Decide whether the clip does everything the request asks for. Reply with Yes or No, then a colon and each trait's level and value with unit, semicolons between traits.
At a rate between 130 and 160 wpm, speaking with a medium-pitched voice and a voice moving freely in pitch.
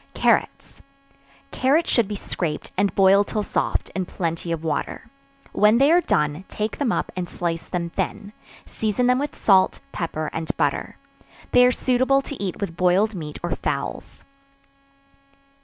No: average, 155 wpm; high, 195 Hz; wide, 6.4 semitones